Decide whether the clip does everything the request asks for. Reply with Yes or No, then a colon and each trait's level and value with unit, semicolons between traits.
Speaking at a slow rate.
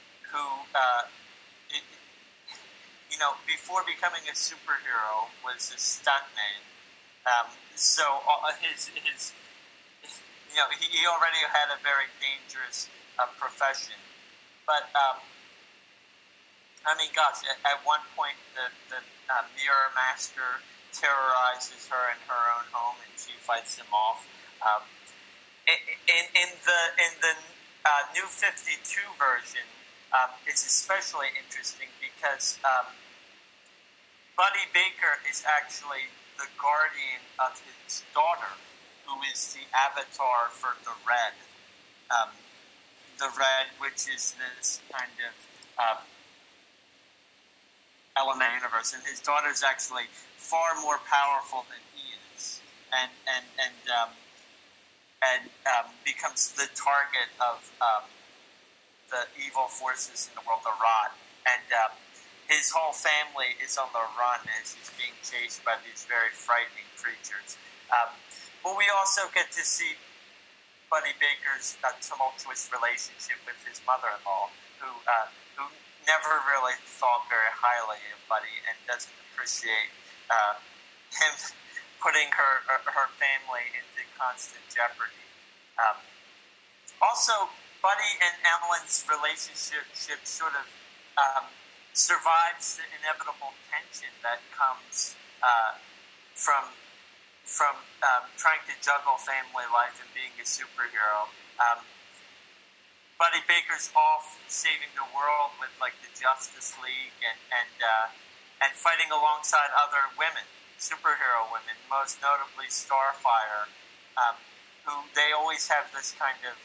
Yes: slow, 125 wpm